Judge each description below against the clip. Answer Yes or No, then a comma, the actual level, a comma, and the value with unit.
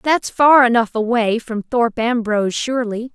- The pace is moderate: Yes, average, 155 wpm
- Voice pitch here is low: No, high, 235 Hz